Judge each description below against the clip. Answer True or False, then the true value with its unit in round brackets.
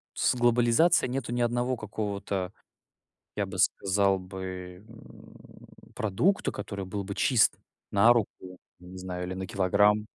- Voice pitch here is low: True (100 Hz)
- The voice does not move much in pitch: False (4.2 semitones)